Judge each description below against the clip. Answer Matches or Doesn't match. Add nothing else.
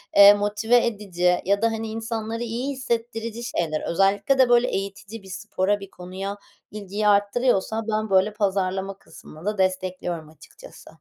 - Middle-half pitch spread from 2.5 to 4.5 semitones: Matches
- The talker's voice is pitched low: Doesn't match